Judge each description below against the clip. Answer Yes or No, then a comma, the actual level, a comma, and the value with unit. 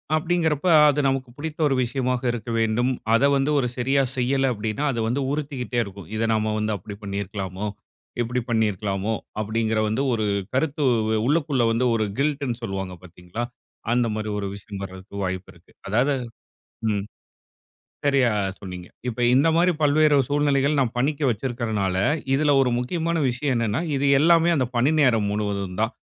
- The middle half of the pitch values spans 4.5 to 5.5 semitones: Yes, average, 4.9 semitones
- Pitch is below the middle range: Yes, low, 120 Hz